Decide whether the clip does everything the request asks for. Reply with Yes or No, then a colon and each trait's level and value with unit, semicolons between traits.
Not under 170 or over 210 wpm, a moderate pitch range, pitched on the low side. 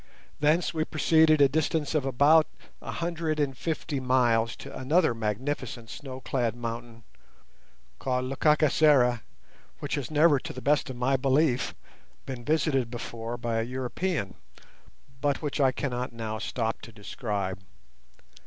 No: average, 140 wpm; average, 4.1 semitones; low, 130 Hz